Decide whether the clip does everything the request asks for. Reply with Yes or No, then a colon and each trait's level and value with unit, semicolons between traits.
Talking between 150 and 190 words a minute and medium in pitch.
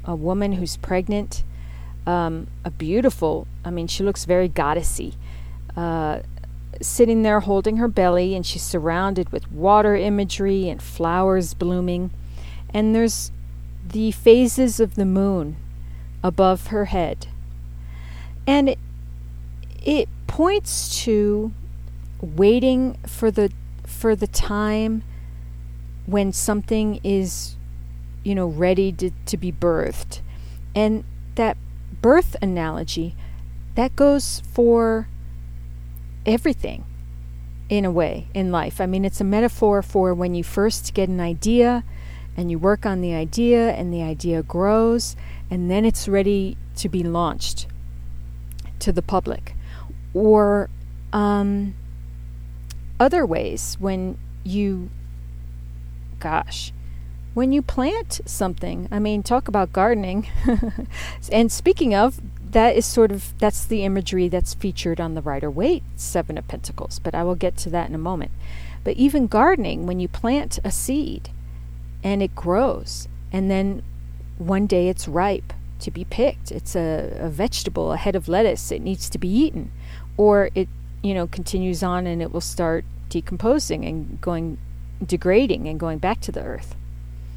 No: slow, 135 wpm; medium, 170 Hz